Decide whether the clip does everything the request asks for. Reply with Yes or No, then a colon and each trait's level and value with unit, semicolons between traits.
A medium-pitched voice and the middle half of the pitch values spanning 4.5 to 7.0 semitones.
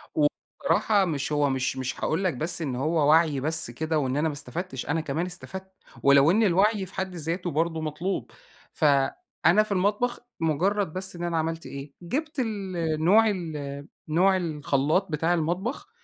No: medium, 165 Hz; average, 4.1 semitones